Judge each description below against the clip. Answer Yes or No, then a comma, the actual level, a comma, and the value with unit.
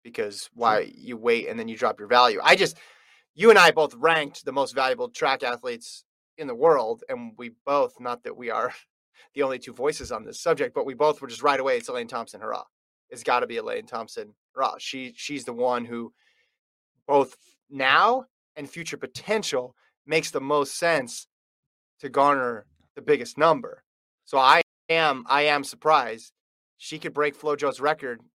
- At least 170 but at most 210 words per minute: Yes, average, 180 wpm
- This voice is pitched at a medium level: Yes, medium, 155 Hz